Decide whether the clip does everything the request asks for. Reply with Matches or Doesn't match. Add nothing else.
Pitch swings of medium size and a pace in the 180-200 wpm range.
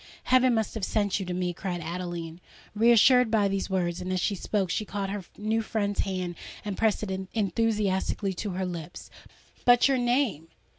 Matches